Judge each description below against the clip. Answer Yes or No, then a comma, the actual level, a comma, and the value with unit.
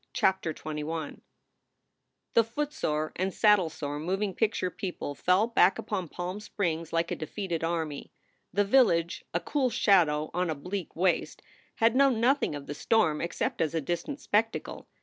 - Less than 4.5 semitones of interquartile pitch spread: No, average, 4.9 semitones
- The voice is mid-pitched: Yes, medium, 180 Hz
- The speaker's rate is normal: Yes, average, 150 wpm